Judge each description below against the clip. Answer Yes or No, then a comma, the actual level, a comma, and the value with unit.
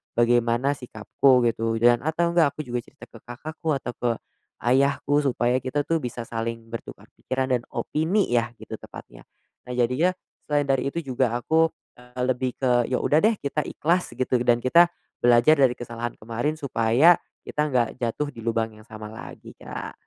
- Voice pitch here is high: No, low, 125 Hz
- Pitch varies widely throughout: No, average, 3.6 semitones